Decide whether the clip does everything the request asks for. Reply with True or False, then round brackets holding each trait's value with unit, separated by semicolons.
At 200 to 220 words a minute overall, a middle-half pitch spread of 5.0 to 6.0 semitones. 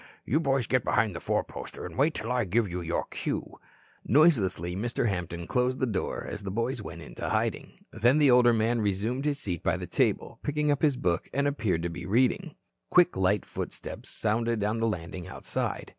True (205 wpm; 5.4 semitones)